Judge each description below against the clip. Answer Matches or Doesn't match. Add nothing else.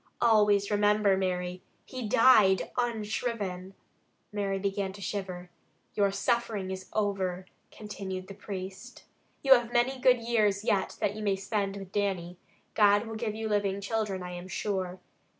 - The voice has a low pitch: Doesn't match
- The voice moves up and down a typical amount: Doesn't match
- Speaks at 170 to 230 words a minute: Doesn't match